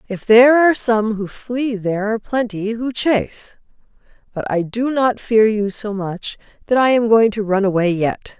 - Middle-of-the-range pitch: No, high, 220 Hz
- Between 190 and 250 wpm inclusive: Yes, average, 195 wpm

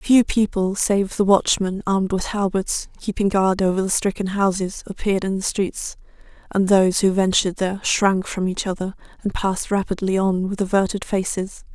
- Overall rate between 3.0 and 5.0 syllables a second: No, 5.2 syllables/s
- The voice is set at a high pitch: Yes, high, 195 Hz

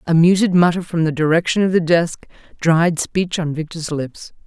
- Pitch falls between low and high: Yes, medium, 170 Hz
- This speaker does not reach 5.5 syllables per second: Yes, 4.9 syllables/s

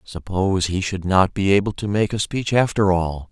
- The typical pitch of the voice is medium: No, very low, 95 Hz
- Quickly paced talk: Yes, fast, 215 wpm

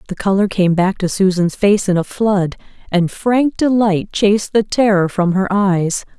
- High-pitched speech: Yes, high, 195 Hz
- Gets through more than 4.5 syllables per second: No, 4.4 syllables/s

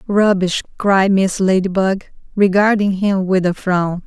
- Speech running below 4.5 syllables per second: Yes, 4.1 syllables/s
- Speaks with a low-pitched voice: No, high, 190 Hz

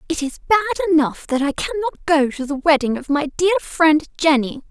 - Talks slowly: No, fast, 205 wpm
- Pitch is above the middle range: Yes, very high, 305 Hz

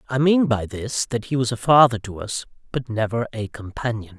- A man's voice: Yes, male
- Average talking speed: No, fast, 215 wpm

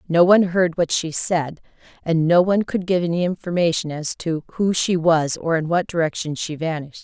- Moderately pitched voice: Yes, medium, 170 Hz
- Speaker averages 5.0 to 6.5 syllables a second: Yes, 5.4 syllables/s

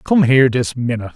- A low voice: Yes, low, 125 Hz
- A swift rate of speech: Yes, fast, 210 wpm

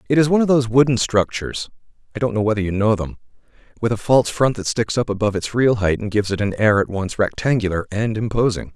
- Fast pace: Yes, fast, 225 wpm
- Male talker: Yes, male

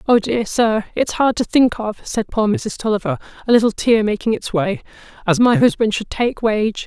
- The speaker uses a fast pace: Yes, fast, 210 wpm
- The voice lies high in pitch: Yes, high, 225 Hz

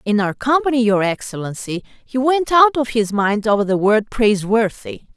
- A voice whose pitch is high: Yes, high, 225 Hz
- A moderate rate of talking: Yes, average, 175 wpm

